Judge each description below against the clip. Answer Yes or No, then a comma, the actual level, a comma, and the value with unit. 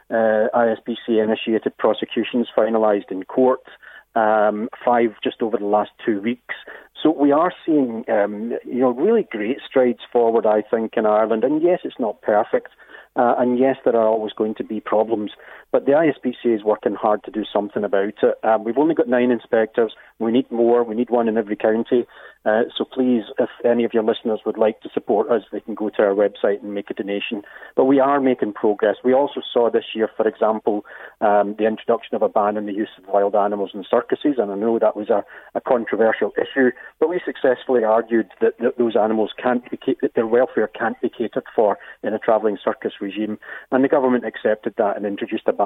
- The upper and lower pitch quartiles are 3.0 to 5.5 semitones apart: No, narrow, 2.4 semitones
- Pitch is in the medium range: No, low, 115 Hz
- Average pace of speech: No, fast, 210 wpm